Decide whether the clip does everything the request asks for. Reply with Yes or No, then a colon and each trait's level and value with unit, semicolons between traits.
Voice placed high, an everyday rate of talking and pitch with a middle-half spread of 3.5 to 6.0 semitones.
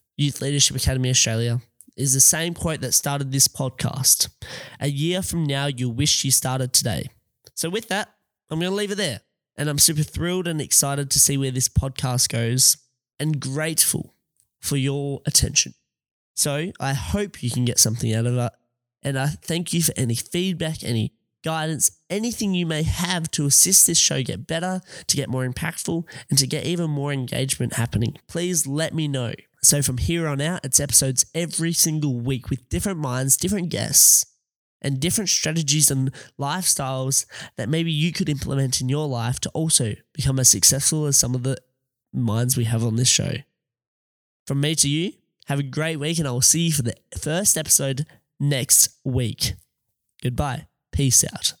No: medium, 140 Hz; average, 180 wpm; average, 4.0 semitones